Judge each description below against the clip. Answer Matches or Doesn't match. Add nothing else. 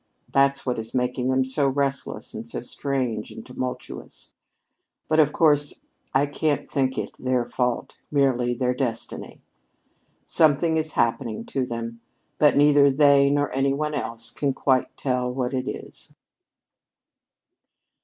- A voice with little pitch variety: Matches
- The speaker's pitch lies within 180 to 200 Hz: Doesn't match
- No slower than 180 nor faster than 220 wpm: Doesn't match